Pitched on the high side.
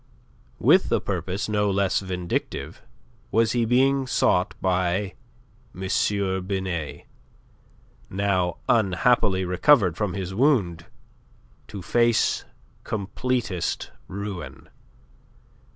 No: low, 100 Hz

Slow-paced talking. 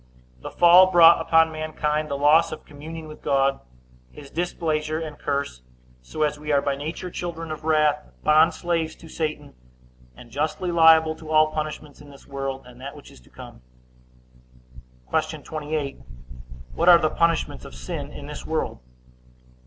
No: average, 165 wpm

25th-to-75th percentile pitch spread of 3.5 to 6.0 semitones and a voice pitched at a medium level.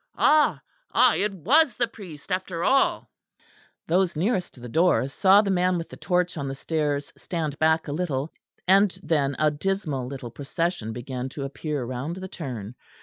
Yes: average, 5.2 semitones; medium, 160 Hz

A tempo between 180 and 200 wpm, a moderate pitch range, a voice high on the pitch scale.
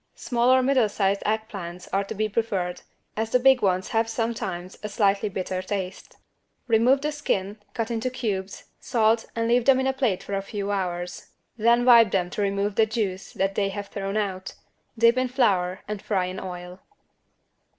Yes: average, 190 wpm; average, 3.5 semitones; high, 210 Hz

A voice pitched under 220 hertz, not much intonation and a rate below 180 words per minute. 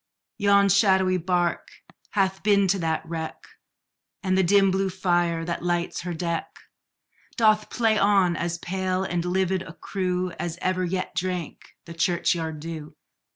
Yes: medium, 185 Hz; narrow, 1.9 semitones; average, 150 wpm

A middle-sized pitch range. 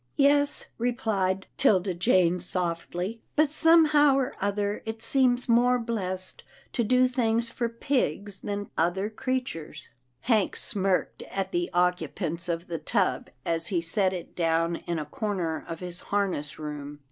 No: wide, 5.8 semitones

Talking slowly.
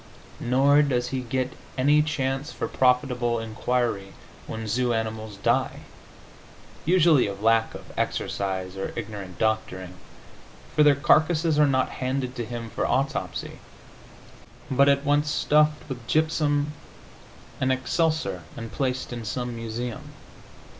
Yes: slow, 125 wpm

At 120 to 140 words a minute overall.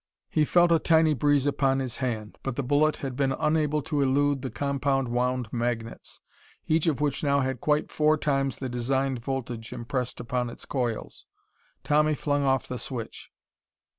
No: average, 170 wpm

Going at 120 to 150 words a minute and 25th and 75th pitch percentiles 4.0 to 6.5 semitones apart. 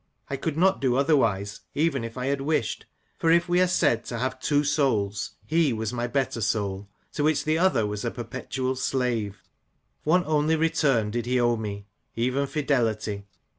No: average, 180 wpm; average, 5.3 semitones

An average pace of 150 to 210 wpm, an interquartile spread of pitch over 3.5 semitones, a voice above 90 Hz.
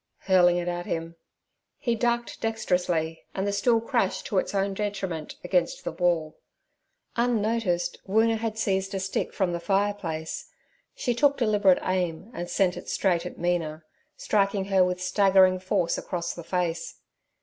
No: average, 160 wpm; average, 2.8 semitones; high, 190 Hz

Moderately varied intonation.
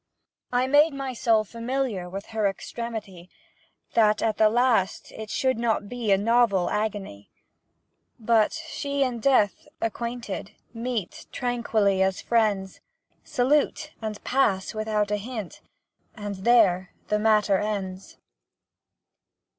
Yes: average, 3.3 semitones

